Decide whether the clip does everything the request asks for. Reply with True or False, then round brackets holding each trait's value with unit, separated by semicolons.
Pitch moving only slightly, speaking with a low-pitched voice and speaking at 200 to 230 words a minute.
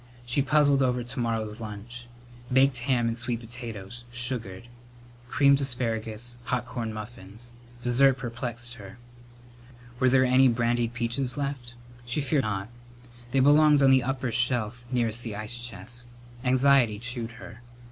False (2.1 semitones; 120 Hz; 145 wpm)